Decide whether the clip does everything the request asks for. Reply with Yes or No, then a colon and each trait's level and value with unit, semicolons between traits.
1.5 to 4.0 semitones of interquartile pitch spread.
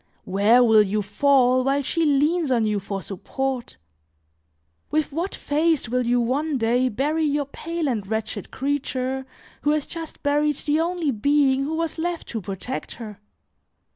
No: average, 4.5 semitones